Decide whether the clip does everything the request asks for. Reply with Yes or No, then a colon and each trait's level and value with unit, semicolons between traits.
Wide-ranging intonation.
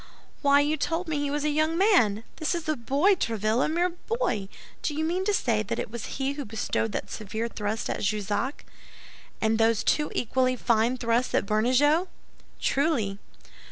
Yes: wide, 5.9 semitones